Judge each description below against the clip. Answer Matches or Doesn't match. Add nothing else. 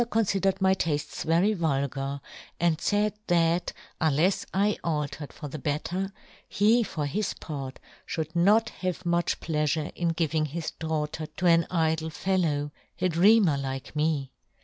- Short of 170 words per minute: Matches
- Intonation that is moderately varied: Matches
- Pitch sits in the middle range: Matches